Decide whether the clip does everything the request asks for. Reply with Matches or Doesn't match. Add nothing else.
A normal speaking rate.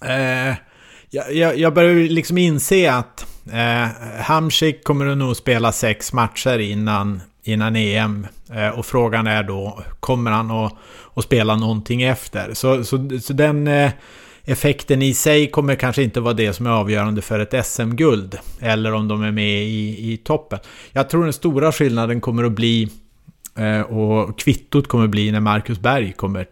Matches